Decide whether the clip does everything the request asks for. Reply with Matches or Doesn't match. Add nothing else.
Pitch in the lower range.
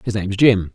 Matches